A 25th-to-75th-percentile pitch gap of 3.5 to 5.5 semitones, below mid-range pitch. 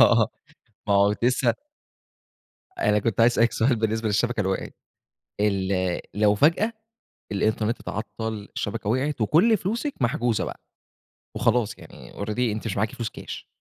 No: average, 2.9 semitones; low, 110 Hz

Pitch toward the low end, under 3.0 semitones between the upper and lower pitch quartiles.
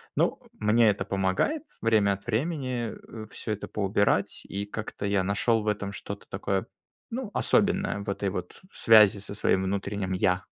Yes: low, 100 Hz; narrow, 2.4 semitones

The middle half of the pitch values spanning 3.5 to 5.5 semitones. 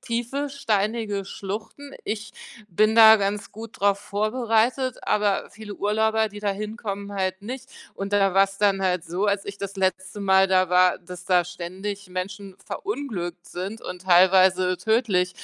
No: average, 2.7 semitones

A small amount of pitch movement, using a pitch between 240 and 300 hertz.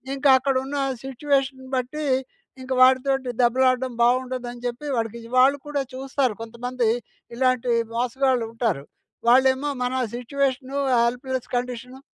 Yes: narrow, 1.6 semitones; very high, 255 Hz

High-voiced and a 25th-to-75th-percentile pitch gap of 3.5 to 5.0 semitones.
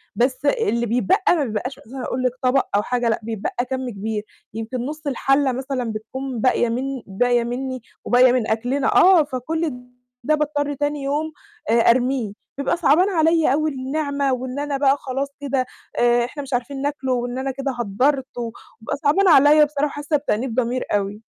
No: very high, 265 Hz; average, 3.0 semitones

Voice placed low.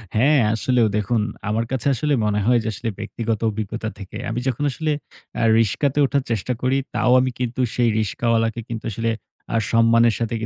Yes: low, 115 Hz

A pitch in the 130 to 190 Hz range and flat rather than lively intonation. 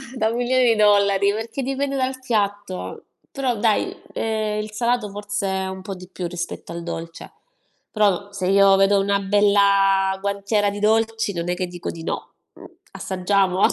No: high, 200 Hz; narrow, 2.3 semitones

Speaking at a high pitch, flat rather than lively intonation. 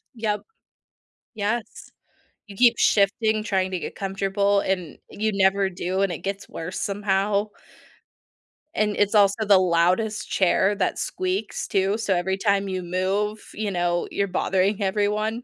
Yes: high, 200 Hz; narrow, 1.7 semitones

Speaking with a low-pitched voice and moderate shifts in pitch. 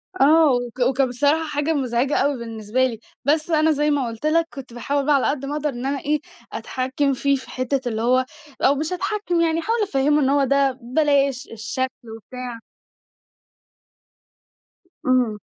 No: very high, 275 Hz; average, 3.0 semitones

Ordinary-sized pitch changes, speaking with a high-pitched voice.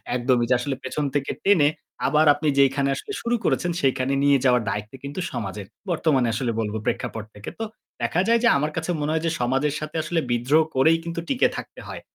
No: average, 4.5 semitones; medium, 140 Hz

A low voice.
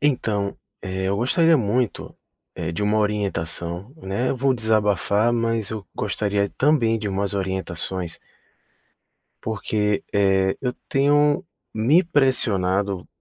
Yes: low, 105 Hz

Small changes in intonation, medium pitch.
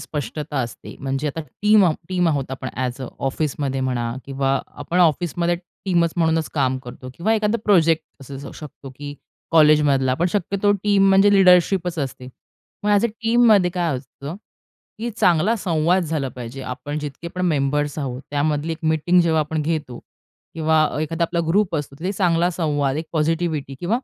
No: average, 4.3 semitones; medium, 160 Hz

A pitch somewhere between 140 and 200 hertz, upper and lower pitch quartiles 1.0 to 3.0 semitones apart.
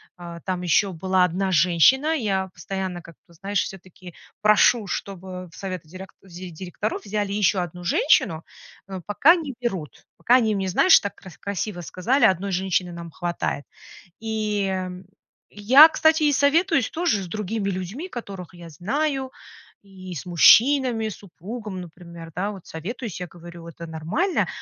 No: high, 190 Hz; average, 4.1 semitones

